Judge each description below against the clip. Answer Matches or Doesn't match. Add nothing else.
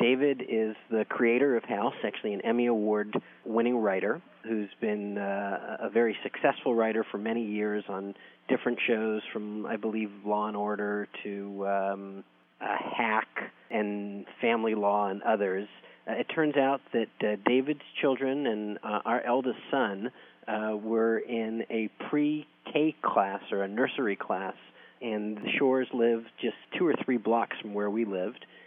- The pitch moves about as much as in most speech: Doesn't match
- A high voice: Doesn't match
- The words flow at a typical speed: Matches